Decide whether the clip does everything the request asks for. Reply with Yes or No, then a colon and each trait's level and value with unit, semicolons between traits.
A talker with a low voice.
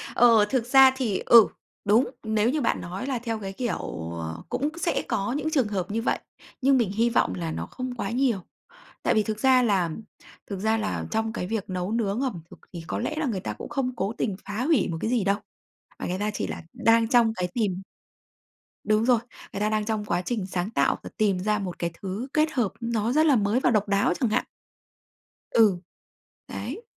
No: high, 220 Hz